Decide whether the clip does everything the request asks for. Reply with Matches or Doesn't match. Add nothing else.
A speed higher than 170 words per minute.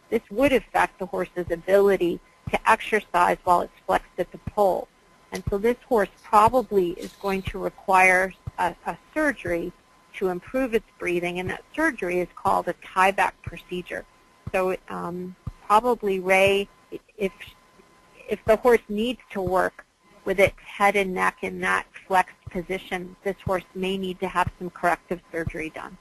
Doesn't match